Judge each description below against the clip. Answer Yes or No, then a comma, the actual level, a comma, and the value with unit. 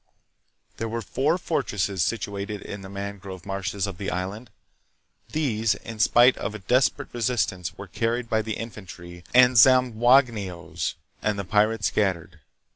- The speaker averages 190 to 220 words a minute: No, average, 145 wpm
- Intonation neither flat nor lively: Yes, average, 3.5 semitones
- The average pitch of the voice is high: No, low, 105 Hz